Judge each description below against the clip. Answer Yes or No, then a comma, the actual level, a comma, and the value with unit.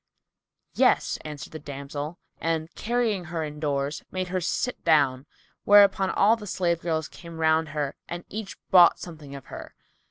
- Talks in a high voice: No, medium, 160 Hz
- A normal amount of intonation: Yes, average, 3.8 semitones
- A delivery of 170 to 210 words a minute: No, average, 155 wpm